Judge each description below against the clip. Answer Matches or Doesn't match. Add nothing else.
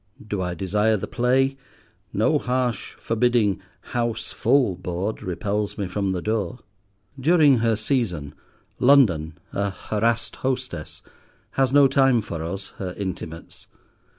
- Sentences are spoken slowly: Matches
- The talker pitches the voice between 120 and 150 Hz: Doesn't match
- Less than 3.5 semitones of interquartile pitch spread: Doesn't match